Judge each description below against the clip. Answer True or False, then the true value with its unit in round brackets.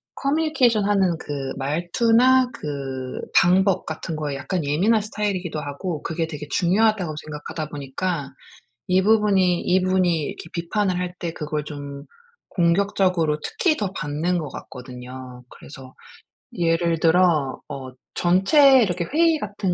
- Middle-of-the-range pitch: True (175 Hz)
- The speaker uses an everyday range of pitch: True (4.9 semitones)